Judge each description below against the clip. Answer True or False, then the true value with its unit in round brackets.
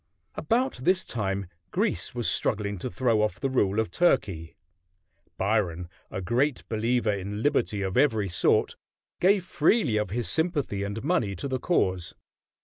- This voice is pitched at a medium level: False (110 Hz)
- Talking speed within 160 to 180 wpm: False (150 wpm)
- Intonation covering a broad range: True (5.9 semitones)